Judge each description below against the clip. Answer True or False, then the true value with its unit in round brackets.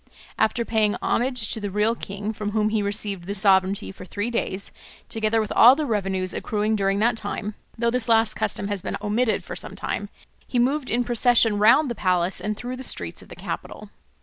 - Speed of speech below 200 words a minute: False (205 wpm)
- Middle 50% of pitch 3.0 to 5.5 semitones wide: False (2.6 semitones)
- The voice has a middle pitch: False (215 Hz)